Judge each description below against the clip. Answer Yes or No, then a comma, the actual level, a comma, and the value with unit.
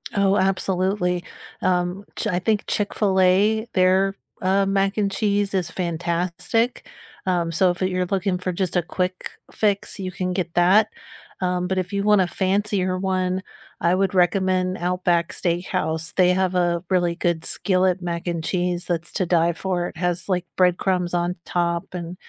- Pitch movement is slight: Yes, narrow, 1.6 semitones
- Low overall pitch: No, medium, 185 Hz